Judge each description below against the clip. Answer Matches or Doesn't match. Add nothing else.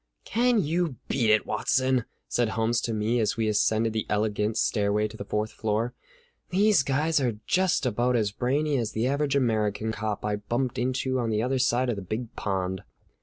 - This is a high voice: Doesn't match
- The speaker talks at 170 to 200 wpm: Matches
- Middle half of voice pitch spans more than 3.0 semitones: Matches